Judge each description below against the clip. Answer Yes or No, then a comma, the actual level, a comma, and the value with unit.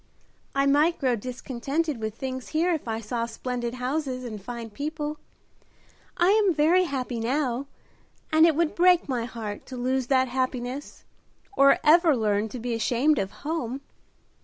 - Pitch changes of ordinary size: Yes, average, 4.3 semitones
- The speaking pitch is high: Yes, very high, 260 Hz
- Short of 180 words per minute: Yes, average, 160 wpm